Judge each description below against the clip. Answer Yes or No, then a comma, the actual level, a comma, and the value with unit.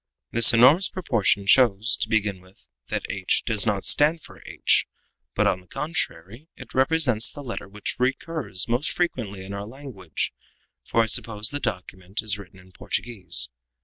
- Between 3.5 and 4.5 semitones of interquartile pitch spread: No, average, 5.2 semitones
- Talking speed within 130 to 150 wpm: No, average, 170 wpm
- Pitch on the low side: Yes, low, 110 Hz